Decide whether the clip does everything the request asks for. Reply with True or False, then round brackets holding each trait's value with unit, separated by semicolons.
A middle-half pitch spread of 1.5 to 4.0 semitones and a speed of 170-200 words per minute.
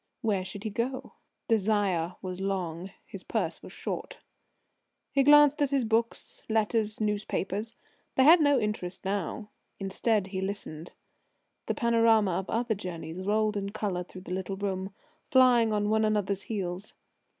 False (3.1 semitones; 150 wpm)